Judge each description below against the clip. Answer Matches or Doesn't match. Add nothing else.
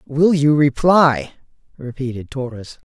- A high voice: Doesn't match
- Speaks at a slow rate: Matches